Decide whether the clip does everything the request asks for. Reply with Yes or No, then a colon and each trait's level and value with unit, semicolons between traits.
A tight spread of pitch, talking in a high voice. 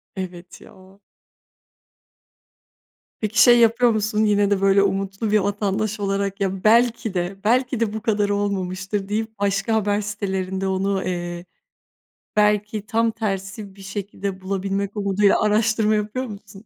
Yes: narrow, 1.8 semitones; high, 200 Hz